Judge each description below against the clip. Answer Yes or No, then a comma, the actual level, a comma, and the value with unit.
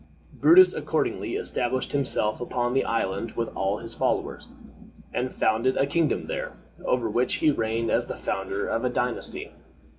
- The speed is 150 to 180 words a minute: Yes, average, 155 wpm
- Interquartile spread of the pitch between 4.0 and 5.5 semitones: No, average, 2.7 semitones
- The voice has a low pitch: Yes, low, 120 Hz